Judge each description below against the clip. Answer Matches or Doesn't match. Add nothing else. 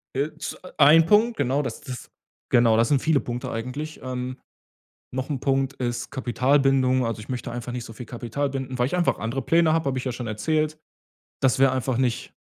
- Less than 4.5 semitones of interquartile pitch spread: Matches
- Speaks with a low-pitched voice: Matches